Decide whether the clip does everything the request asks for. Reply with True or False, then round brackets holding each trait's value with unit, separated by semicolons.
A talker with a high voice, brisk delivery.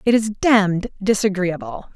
False (200 Hz; 125 wpm)